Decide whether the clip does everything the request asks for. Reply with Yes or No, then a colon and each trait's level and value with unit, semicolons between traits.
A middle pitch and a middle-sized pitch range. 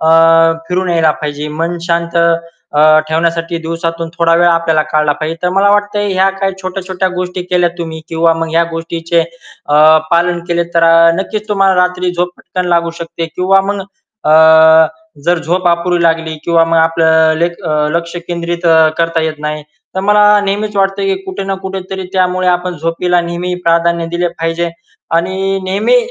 No: medium, 170 Hz; narrow, 1.8 semitones